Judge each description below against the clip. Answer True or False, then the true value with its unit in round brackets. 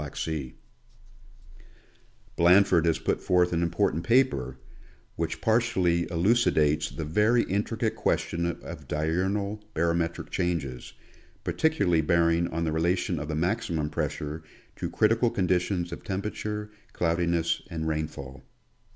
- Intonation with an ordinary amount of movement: True (3.9 semitones)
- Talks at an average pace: False (125 wpm)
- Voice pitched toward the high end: False (85 Hz)